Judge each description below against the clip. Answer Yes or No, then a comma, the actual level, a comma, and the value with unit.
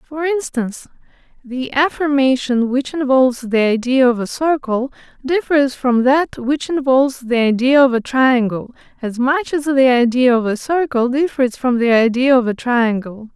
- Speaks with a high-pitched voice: Yes, very high, 260 Hz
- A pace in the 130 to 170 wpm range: Yes, average, 160 wpm